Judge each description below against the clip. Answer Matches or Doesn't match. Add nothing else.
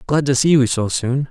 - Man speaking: Matches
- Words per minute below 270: Doesn't match